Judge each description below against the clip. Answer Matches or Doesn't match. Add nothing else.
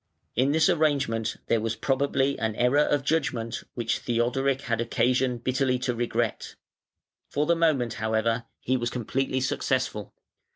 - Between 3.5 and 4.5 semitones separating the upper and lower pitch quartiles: Doesn't match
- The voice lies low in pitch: Matches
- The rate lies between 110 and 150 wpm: Matches